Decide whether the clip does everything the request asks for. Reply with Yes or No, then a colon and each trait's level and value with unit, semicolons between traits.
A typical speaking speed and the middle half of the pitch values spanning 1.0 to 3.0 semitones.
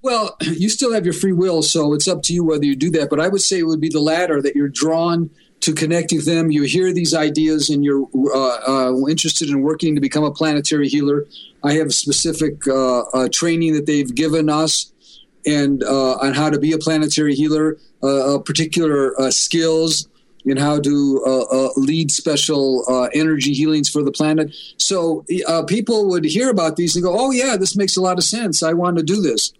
No: fast, 220 wpm; narrow, 2.5 semitones